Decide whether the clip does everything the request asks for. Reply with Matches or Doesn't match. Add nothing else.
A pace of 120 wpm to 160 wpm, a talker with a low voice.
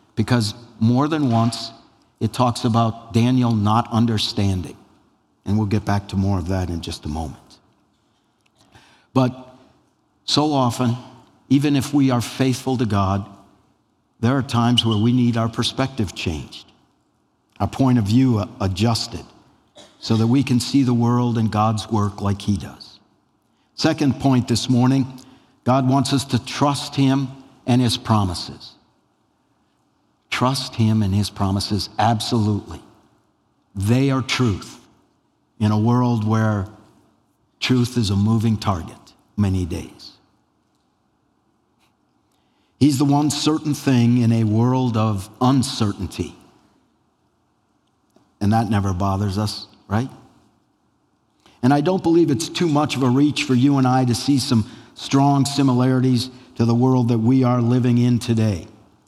Matches